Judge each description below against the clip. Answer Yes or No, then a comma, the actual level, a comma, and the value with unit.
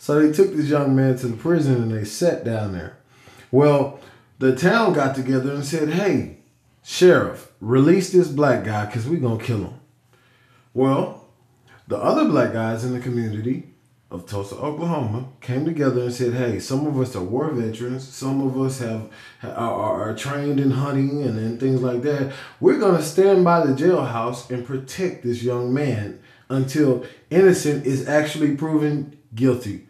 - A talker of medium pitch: No, low, 130 Hz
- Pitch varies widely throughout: No, average, 3.5 semitones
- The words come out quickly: No, average, 175 wpm